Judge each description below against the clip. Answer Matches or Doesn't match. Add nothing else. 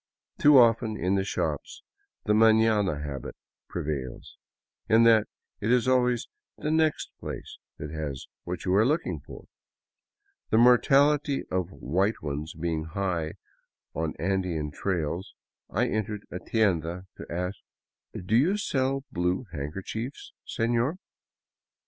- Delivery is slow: Matches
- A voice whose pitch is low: Matches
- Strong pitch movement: Matches